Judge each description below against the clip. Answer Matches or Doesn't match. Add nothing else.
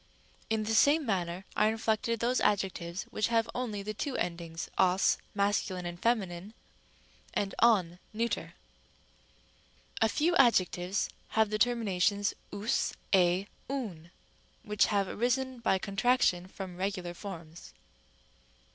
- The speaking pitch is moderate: Doesn't match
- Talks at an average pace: Doesn't match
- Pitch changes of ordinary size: Matches